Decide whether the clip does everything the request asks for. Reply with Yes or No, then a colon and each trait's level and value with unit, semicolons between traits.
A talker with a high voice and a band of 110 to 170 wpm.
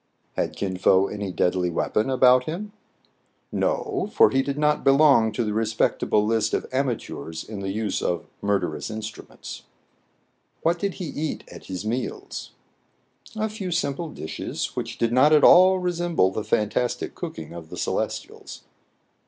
No: low, 120 Hz; average, 165 wpm